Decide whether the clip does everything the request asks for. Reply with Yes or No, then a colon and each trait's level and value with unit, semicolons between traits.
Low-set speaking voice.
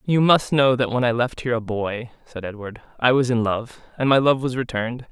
Yes: low, 125 Hz